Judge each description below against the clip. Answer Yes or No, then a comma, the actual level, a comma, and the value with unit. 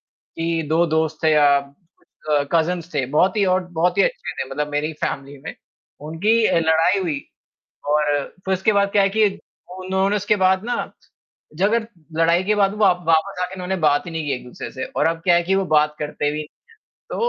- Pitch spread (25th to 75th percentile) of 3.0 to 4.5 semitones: Yes, average, 4.2 semitones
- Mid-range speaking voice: Yes, medium, 170 Hz